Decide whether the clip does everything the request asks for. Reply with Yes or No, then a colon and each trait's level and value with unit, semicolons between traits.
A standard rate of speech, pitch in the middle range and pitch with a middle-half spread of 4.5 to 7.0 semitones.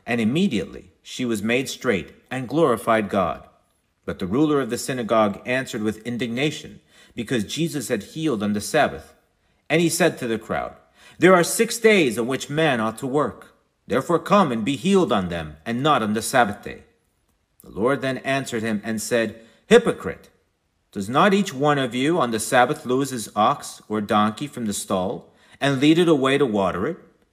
No: average, 190 wpm; low, 125 Hz; wide, 5.6 semitones